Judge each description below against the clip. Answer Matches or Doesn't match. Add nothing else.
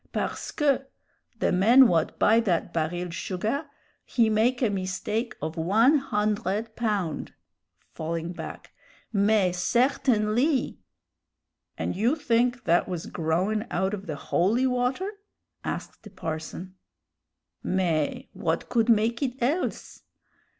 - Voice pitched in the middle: Doesn't match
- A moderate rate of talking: Doesn't match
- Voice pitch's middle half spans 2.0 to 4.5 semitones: Doesn't match